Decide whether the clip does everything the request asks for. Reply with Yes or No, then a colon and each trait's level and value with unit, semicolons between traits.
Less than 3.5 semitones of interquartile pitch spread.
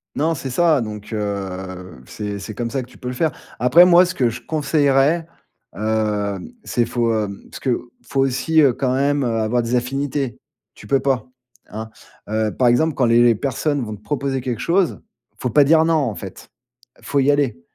No: average, 4.6 semitones